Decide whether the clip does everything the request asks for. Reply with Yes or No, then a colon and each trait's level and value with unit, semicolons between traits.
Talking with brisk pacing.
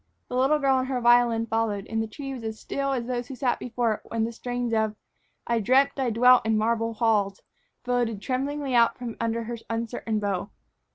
Yes: fast, 210 wpm